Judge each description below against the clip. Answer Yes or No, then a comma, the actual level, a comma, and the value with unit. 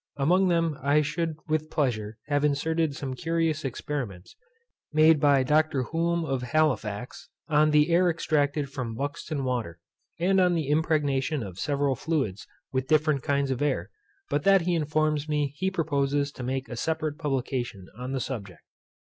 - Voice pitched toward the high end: No, medium, 145 Hz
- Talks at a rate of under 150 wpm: No, average, 160 wpm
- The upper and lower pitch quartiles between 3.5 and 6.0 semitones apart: No, average, 3.1 semitones